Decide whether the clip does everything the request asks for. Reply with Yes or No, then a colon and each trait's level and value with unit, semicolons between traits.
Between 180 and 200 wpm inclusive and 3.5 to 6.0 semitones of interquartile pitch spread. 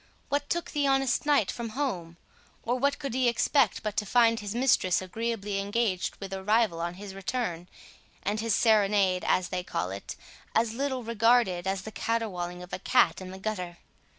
Yes: average, 185 wpm; average, 4.4 semitones